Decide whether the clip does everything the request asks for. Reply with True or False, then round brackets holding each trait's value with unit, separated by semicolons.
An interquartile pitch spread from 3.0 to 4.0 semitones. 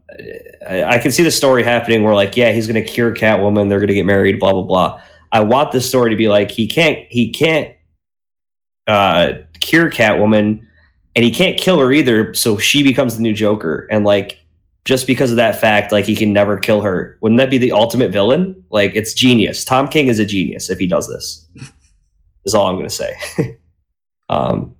False (4.5 semitones)